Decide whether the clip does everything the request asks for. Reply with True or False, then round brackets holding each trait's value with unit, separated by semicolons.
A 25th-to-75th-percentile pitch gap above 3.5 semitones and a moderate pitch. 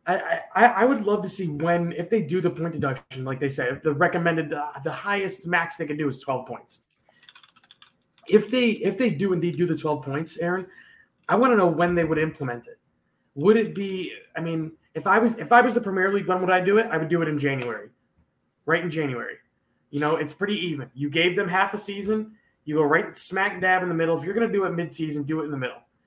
True (4.2 semitones; 170 Hz)